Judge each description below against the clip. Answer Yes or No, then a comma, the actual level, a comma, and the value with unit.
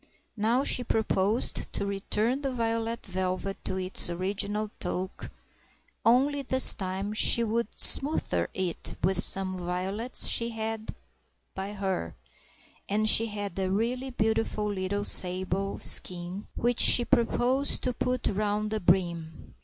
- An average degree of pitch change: Yes, average, 3.6 semitones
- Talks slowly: Yes, slow, 130 wpm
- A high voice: Yes, high, 205 Hz